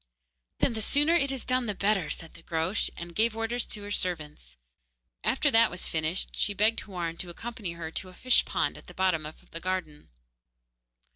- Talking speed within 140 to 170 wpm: No, average, 200 wpm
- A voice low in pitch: No, high, 190 Hz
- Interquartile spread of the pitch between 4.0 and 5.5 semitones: Yes, average, 5.2 semitones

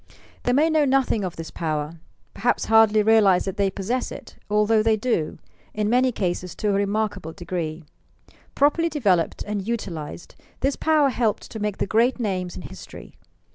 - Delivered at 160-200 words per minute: Yes, average, 175 wpm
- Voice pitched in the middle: No, high, 210 Hz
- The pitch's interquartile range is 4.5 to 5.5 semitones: Yes, average, 4.9 semitones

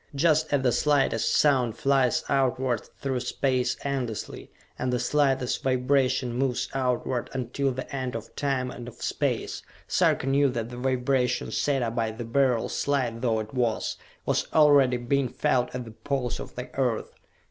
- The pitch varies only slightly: Yes, narrow, 2.0 semitones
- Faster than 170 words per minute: No, average, 165 wpm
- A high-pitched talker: No, low, 130 Hz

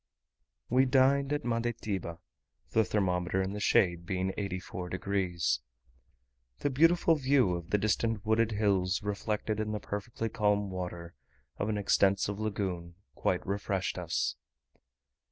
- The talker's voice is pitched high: No, low, 100 Hz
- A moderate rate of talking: No, slow, 130 wpm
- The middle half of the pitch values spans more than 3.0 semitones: Yes, average, 3.4 semitones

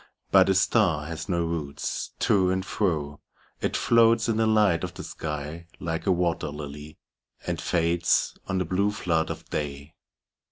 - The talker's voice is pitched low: Yes, very low, 85 Hz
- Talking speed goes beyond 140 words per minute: Yes, average, 165 wpm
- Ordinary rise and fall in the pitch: Yes, average, 3.7 semitones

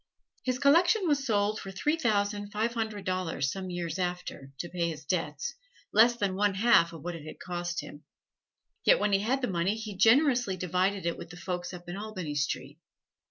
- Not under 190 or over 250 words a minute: Yes, average, 195 wpm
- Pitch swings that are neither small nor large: Yes, average, 4.1 semitones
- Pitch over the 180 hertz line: Yes, high, 190 Hz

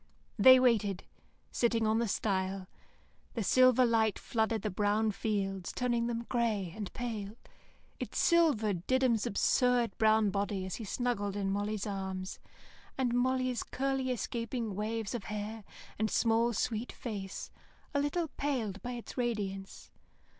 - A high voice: Yes, high, 220 Hz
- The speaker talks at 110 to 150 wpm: Yes, average, 140 wpm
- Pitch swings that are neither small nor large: Yes, average, 3.3 semitones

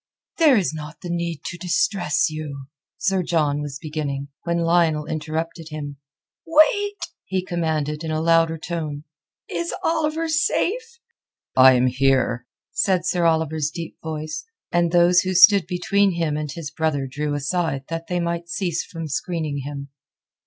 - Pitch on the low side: No, medium, 165 Hz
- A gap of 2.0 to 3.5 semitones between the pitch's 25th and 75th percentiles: Yes, average, 2.9 semitones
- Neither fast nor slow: Yes, average, 150 wpm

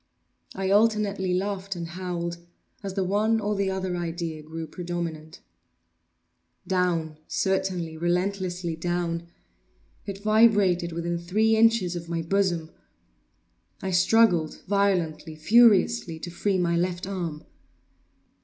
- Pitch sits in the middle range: Yes, medium, 180 Hz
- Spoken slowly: Yes, slow, 110 wpm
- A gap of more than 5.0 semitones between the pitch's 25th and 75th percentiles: No, average, 2.7 semitones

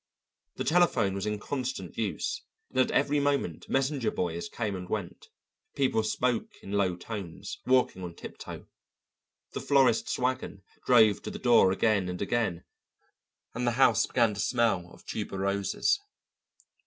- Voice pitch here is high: No, low, 110 Hz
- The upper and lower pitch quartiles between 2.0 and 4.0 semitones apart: No, average, 4.9 semitones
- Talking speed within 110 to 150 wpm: Yes, average, 145 wpm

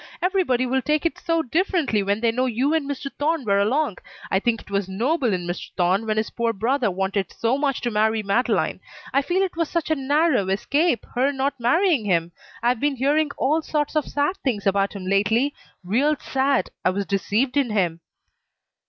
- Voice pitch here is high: Yes, very high, 250 Hz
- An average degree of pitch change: No, wide, 6.3 semitones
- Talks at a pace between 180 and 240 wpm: Yes, average, 200 wpm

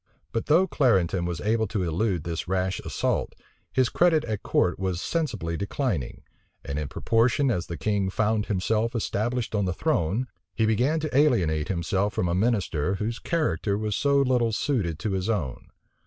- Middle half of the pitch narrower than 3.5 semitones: No, average, 5.1 semitones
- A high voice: No, low, 105 Hz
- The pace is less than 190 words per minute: Yes, average, 170 wpm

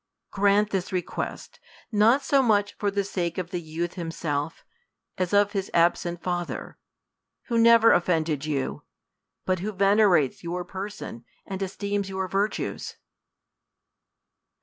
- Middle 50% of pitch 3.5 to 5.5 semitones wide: No, average, 3.0 semitones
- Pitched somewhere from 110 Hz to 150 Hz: No, high, 190 Hz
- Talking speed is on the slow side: Yes, slow, 125 wpm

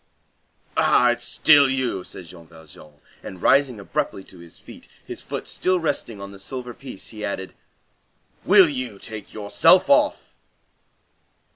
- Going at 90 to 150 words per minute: Yes, average, 145 wpm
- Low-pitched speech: Yes, low, 110 Hz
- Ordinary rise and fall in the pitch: No, wide, 5.7 semitones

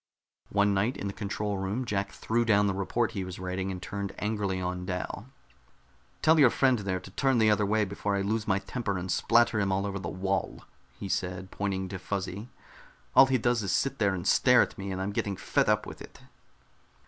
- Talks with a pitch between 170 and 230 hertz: No, low, 100 Hz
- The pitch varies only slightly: Yes, narrow, 2.3 semitones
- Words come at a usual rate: No, fast, 220 wpm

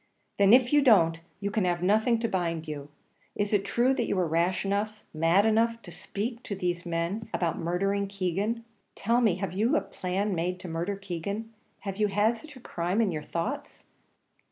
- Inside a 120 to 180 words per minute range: No, average, 200 wpm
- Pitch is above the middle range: Yes, high, 195 Hz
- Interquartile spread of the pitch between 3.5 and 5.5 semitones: Yes, average, 4.0 semitones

